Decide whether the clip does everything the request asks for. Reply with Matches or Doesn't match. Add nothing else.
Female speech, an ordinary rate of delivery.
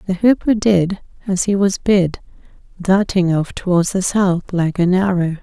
Matches